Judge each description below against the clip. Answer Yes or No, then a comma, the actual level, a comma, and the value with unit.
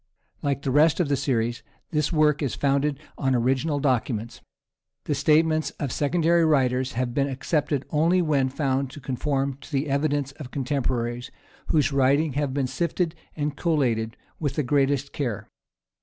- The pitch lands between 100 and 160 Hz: Yes, medium, 140 Hz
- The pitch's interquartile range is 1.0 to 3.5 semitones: Yes, narrow, 2.5 semitones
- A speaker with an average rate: Yes, average, 155 wpm